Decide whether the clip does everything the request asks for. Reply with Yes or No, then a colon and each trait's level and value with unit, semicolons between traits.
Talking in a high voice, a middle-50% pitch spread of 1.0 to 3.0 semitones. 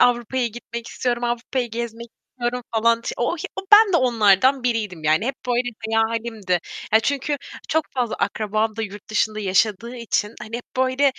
Yes: high, 235 Hz; narrow, 2.5 semitones